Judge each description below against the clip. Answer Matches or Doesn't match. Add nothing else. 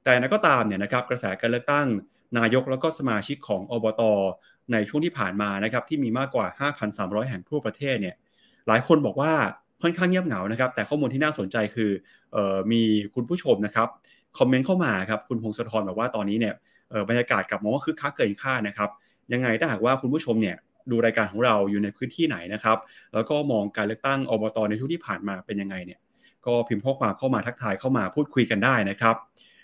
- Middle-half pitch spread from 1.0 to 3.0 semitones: Doesn't match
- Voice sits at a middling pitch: Doesn't match